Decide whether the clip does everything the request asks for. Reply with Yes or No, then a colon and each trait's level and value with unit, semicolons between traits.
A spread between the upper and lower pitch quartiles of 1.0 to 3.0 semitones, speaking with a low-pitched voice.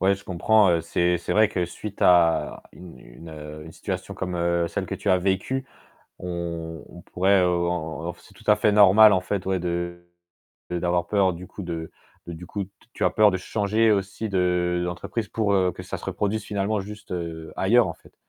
Yes: narrow, 2.6 semitones; very low, 90 Hz